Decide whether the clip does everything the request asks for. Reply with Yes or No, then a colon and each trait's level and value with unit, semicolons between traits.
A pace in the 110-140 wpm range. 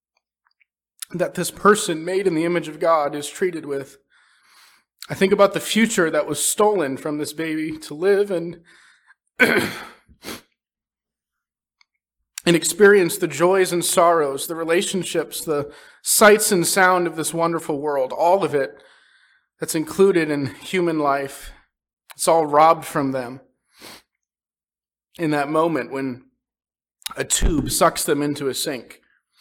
Yes: slow, 135 wpm